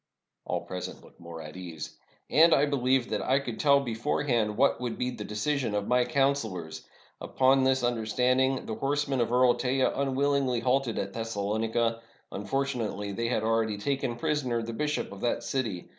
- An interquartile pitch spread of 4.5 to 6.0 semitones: No, average, 3.7 semitones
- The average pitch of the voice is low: Yes, low, 120 Hz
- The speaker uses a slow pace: No, average, 175 wpm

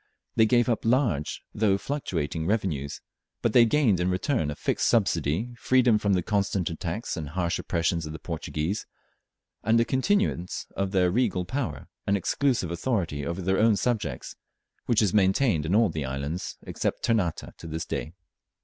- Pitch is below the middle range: Yes, very low, 95 Hz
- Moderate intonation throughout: No, wide, 5.7 semitones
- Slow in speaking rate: No, average, 165 wpm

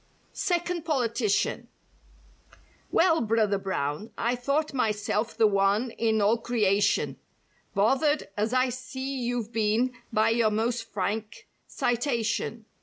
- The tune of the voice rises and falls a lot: No, average, 3.2 semitones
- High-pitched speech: Yes, high, 230 Hz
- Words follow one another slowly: Yes, slow, 115 wpm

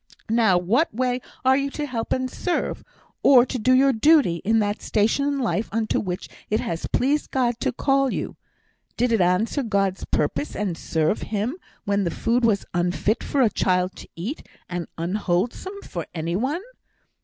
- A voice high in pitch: Yes, high, 225 Hz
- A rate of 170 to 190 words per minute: Yes, average, 180 wpm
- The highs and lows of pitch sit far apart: Yes, wide, 6.0 semitones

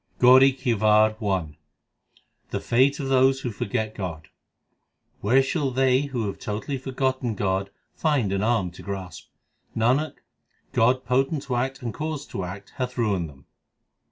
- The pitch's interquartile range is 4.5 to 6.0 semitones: Yes, average, 4.9 semitones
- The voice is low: Yes, low, 120 Hz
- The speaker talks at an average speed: Yes, average, 155 wpm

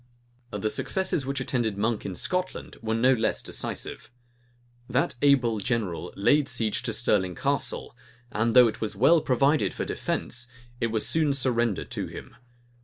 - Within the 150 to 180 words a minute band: Yes, average, 155 wpm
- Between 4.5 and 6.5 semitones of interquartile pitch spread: No, average, 3.6 semitones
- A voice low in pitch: Yes, low, 120 Hz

